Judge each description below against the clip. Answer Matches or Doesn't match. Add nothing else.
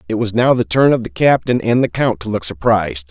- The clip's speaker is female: Doesn't match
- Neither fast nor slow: Doesn't match